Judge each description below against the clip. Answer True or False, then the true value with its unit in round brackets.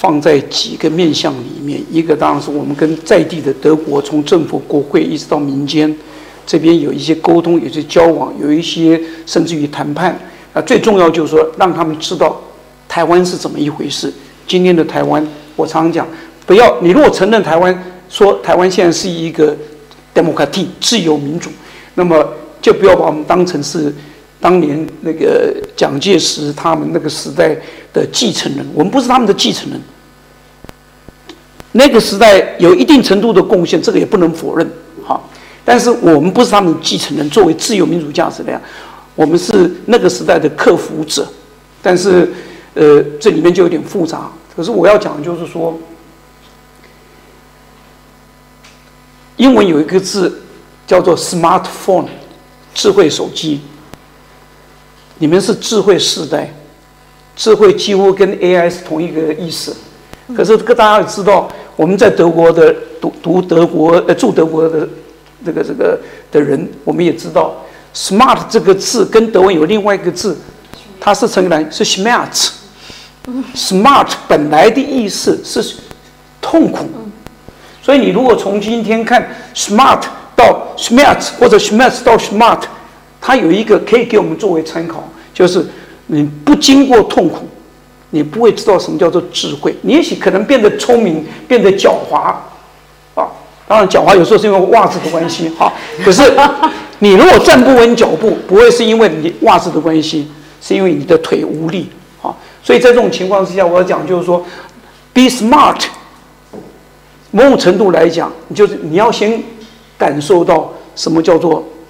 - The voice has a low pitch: False (180 Hz)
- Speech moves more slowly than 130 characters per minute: False (270 characters per minute)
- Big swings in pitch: True (6.4 semitones)